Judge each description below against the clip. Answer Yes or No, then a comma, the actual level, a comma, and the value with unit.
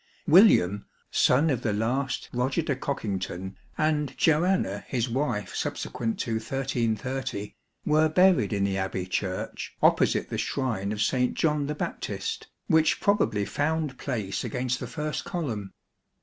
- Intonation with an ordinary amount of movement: No, wide, 6.4 semitones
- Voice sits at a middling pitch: No, low, 125 Hz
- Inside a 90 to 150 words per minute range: Yes, slow, 135 wpm